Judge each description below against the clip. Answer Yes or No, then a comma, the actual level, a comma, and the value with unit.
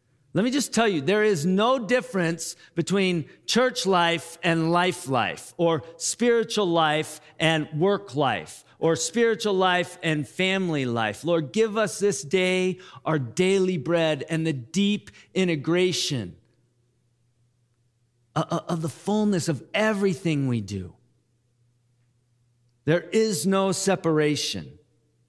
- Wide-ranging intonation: Yes, wide, 6.3 semitones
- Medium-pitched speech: Yes, medium, 165 Hz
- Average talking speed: No, slow, 120 wpm